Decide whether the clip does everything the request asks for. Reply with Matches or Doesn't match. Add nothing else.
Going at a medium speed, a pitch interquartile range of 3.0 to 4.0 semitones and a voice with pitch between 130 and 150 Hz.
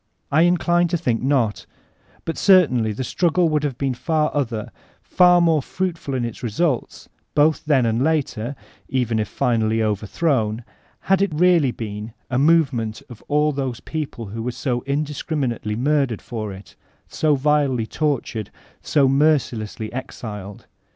Doesn't match